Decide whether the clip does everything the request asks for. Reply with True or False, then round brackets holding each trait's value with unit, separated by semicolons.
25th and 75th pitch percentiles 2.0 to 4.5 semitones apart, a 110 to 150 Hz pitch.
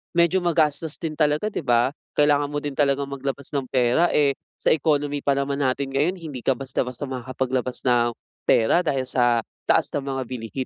True (2.4 semitones; 140 Hz)